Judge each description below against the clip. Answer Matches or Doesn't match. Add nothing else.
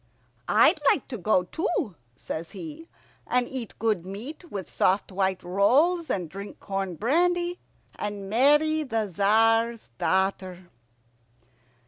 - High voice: Matches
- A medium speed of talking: Doesn't match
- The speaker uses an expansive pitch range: Matches